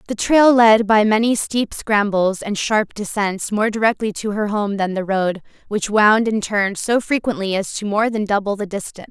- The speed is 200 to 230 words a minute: Yes, fast, 205 wpm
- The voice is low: No, high, 210 Hz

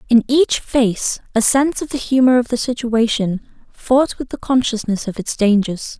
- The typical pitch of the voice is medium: No, high, 240 Hz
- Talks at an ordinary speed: Yes, average, 180 wpm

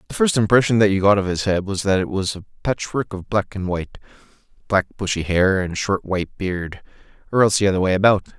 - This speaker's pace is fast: Yes, fast, 220 wpm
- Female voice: No, male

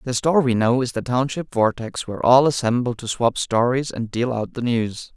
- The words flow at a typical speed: No, fast, 220 wpm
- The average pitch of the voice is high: No, low, 125 Hz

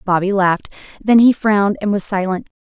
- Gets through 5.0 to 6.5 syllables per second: Yes, 5.7 syllables/s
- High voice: Yes, high, 200 Hz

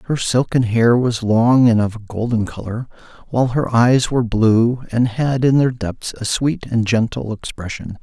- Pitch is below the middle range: Yes, low, 120 Hz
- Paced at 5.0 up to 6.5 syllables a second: No, 4.7 syllables/s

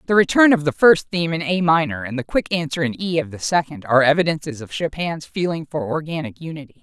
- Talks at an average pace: No, fast, 230 wpm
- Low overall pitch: No, medium, 155 Hz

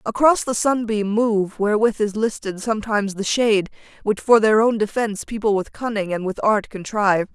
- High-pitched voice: Yes, high, 215 Hz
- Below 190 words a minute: Yes, average, 180 wpm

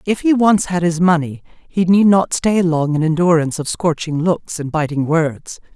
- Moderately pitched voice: Yes, medium, 170 Hz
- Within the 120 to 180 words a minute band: No, average, 200 wpm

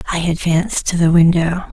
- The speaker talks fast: No, average, 170 wpm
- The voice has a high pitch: No, medium, 170 Hz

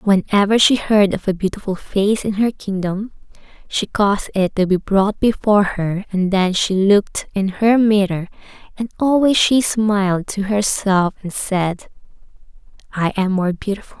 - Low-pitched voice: No, high, 200 Hz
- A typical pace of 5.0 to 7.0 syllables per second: No, 4.5 syllables/s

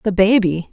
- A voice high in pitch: Yes, high, 195 Hz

